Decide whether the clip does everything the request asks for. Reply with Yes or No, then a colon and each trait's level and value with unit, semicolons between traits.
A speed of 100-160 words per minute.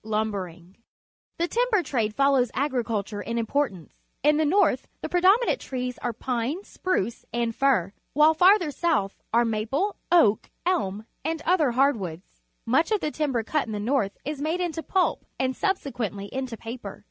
No: average, 170 wpm